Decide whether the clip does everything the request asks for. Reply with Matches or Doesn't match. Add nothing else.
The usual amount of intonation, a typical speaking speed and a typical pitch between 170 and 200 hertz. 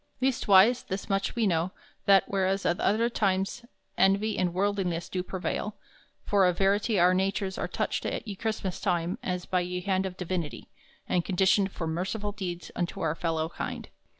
Doesn't match